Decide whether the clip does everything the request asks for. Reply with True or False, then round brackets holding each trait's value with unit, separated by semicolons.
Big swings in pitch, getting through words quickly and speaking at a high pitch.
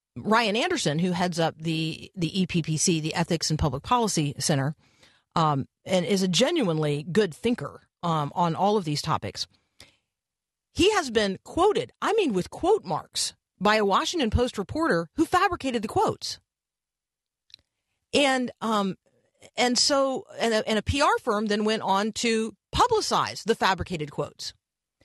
False (6.8 semitones; 145 wpm; 200 Hz)